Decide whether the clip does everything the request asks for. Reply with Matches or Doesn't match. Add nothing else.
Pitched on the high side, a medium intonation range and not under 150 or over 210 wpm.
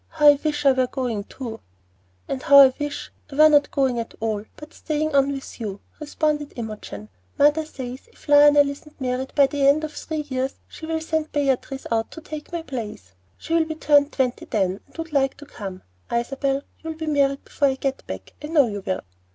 Matches